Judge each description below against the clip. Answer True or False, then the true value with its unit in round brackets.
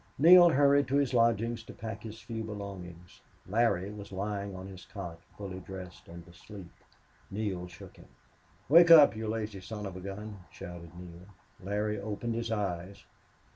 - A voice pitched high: False (100 Hz)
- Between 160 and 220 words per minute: True (165 wpm)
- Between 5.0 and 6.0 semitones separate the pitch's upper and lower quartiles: False (3.5 semitones)